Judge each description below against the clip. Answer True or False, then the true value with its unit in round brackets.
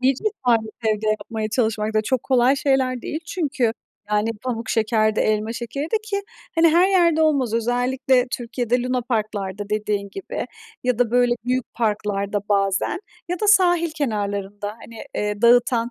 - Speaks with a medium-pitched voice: False (240 Hz)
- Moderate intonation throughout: True (3.8 semitones)